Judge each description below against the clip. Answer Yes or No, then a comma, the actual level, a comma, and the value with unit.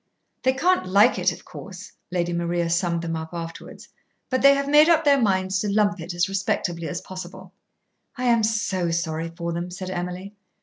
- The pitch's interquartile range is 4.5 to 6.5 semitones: No, average, 4.0 semitones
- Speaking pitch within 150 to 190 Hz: Yes, medium, 185 Hz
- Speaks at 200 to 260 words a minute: No, average, 190 wpm